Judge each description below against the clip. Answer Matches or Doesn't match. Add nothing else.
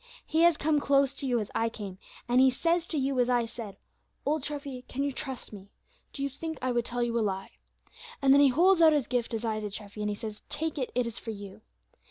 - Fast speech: Matches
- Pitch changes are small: Doesn't match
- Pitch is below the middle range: Doesn't match